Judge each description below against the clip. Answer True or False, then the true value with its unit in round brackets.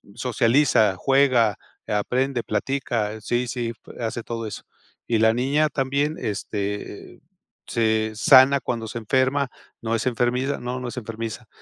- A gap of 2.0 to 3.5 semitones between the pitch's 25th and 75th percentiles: True (3.0 semitones)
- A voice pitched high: False (120 Hz)